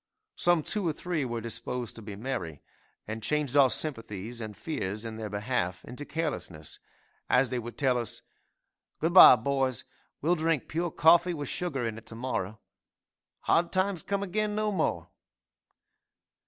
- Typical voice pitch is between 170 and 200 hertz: No, low, 130 Hz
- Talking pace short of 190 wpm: Yes, average, 160 wpm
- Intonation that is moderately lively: No, wide, 6.6 semitones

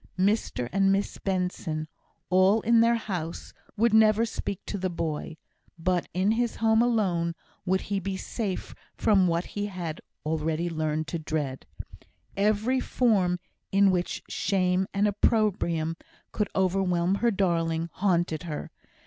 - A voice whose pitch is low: No, medium, 185 Hz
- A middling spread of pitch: Yes, average, 3.6 semitones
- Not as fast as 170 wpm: Yes, average, 140 wpm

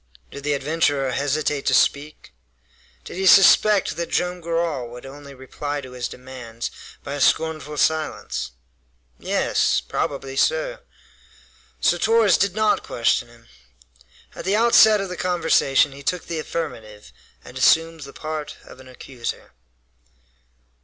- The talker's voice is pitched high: No, medium, 150 Hz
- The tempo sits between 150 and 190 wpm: No, average, 140 wpm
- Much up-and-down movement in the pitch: No, average, 4.8 semitones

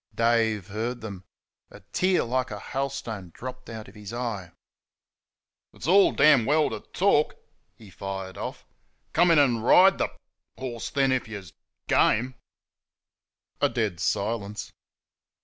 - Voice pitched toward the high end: No, low, 115 Hz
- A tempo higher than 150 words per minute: No, average, 140 wpm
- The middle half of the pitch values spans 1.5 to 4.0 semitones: No, average, 4.6 semitones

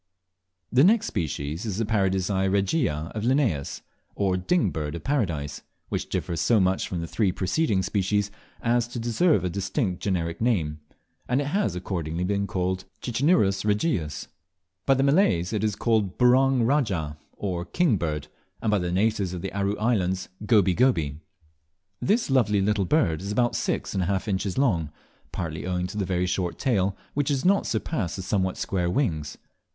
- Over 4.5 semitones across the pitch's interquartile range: Yes, average, 5.1 semitones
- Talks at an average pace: Yes, average, 175 wpm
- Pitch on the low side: Yes, low, 100 Hz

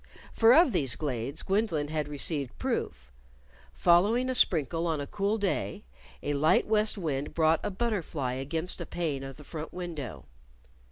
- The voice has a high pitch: No, medium, 160 Hz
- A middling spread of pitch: No, wide, 5.8 semitones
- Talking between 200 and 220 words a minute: No, average, 160 wpm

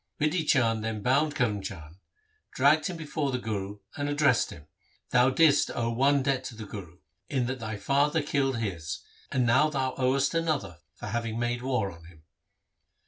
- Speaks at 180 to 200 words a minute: Yes, average, 185 wpm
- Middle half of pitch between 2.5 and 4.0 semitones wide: No, average, 4.8 semitones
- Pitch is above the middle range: No, low, 125 Hz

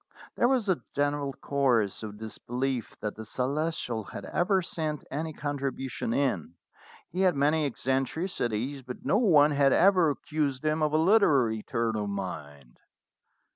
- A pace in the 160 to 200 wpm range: No, average, 145 wpm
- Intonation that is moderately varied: Yes, average, 5.0 semitones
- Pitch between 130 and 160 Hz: Yes, medium, 140 Hz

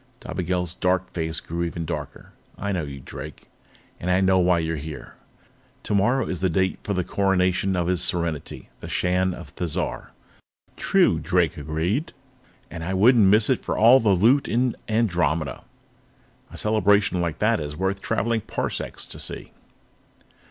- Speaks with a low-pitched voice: Yes, very low, 90 Hz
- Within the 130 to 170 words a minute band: Yes, average, 160 wpm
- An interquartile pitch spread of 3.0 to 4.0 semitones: Yes, average, 3.4 semitones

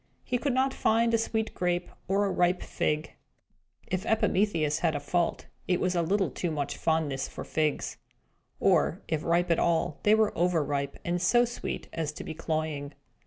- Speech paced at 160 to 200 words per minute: Yes, average, 180 wpm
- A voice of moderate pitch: Yes, medium, 175 Hz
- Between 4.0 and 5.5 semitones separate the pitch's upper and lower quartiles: Yes, average, 4.5 semitones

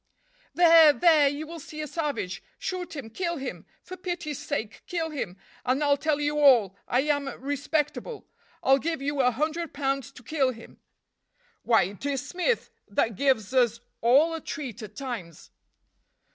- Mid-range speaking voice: No, very high, 285 Hz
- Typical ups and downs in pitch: Yes, average, 4.1 semitones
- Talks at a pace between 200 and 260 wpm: No, average, 165 wpm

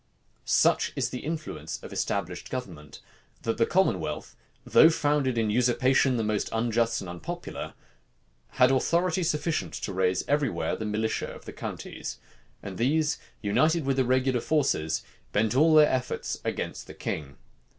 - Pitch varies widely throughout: Yes, wide, 5.8 semitones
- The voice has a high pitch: No, low, 125 Hz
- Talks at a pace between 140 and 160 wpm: Yes, average, 150 wpm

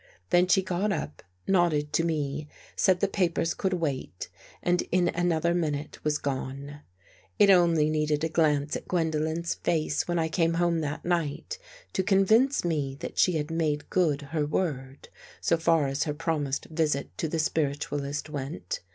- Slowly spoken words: No, average, 165 wpm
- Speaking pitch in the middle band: Yes, medium, 160 Hz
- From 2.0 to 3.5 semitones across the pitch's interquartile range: Yes, average, 2.9 semitones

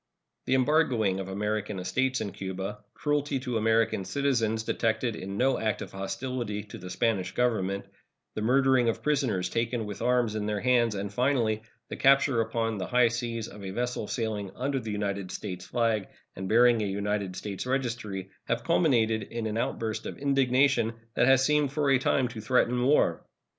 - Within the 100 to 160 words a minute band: No, average, 180 wpm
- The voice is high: No, low, 115 Hz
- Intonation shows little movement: No, average, 3.6 semitones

